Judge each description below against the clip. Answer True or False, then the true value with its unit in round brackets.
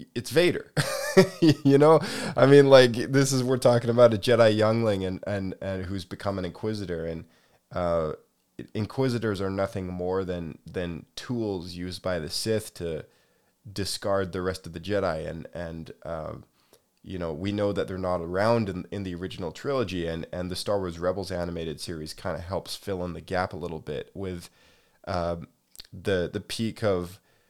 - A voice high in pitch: False (95 Hz)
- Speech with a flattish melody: False (3.6 semitones)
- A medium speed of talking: True (180 wpm)